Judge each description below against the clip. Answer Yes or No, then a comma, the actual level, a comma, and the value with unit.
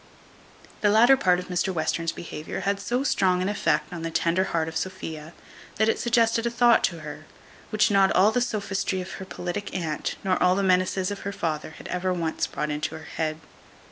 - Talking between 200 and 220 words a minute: Yes, fast, 205 wpm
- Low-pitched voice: No, medium, 185 Hz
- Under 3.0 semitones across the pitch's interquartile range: No, average, 3.5 semitones